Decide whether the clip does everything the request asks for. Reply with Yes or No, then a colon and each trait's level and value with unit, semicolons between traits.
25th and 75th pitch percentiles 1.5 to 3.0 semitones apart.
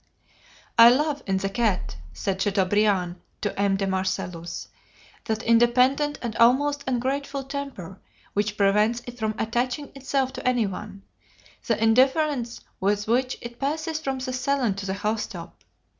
No: average, 4.8 semitones